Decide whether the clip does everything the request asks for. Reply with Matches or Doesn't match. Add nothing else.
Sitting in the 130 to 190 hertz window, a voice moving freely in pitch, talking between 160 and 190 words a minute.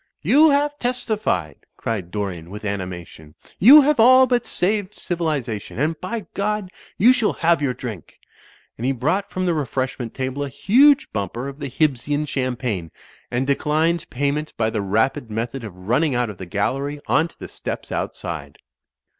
Matches